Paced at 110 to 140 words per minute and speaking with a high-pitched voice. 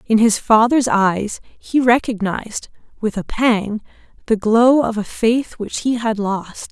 No: average, 160 wpm; high, 225 Hz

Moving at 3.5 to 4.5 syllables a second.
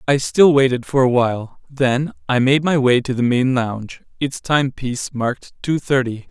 No: 5.0 syllables/s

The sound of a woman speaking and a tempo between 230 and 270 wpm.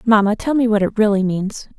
Yes: female; fast, 235 wpm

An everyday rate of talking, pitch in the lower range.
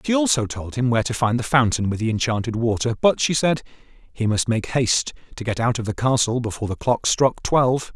No: fast, 235 wpm; low, 120 Hz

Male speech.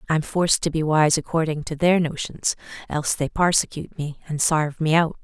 No: female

